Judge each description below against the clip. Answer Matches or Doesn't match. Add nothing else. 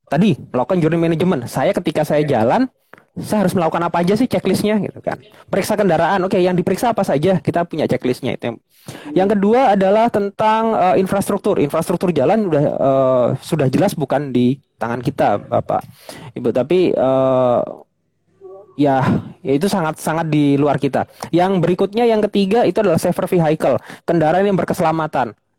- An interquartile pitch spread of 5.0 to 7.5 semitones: Matches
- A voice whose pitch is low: Doesn't match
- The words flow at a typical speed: Doesn't match